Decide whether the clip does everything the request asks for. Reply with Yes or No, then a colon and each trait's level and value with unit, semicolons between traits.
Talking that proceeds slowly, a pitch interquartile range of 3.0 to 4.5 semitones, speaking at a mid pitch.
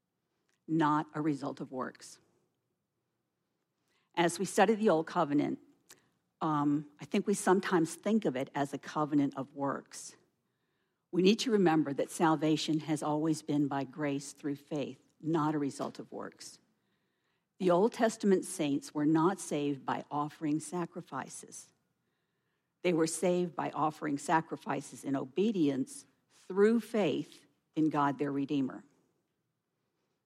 Yes: slow, 130 wpm; average, 4.0 semitones; medium, 155 Hz